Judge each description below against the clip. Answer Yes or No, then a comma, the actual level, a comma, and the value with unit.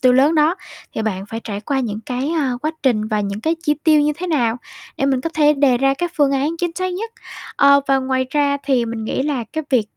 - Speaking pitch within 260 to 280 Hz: Yes, very high, 275 Hz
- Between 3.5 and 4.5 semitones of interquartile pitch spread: Yes, average, 3.8 semitones